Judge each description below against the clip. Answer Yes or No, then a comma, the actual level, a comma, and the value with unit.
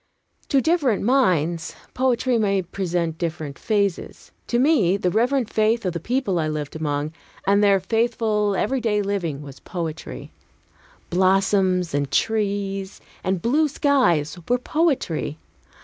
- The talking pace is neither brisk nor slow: No, slow, 130 wpm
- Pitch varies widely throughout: Yes, wide, 5.7 semitones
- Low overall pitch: No, high, 195 Hz